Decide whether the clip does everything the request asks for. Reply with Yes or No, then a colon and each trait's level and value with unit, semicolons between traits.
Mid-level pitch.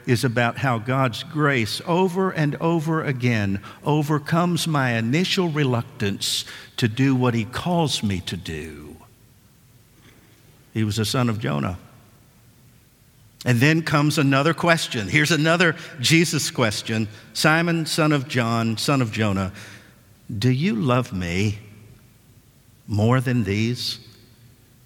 No: low, 125 Hz